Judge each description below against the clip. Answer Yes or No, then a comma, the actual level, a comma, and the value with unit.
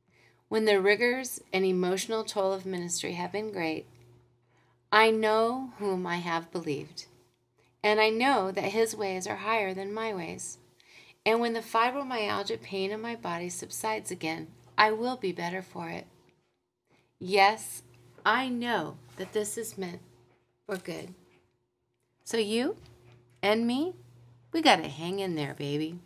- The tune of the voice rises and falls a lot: Yes, wide, 6.9 semitones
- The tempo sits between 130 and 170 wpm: Yes, average, 145 wpm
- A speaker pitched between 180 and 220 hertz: Yes, high, 190 Hz